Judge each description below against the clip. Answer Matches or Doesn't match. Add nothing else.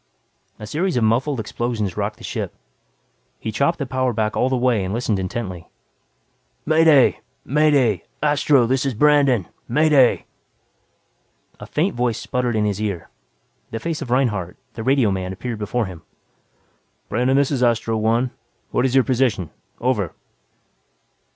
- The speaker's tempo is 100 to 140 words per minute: Doesn't match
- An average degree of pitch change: Matches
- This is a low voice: Matches